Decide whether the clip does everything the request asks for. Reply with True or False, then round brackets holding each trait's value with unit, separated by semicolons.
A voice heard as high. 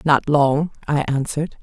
False (145 Hz)